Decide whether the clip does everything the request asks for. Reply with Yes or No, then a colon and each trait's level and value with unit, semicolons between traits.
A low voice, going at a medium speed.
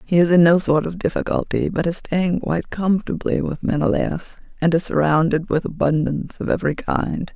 No: medium, 170 Hz; average, 180 wpm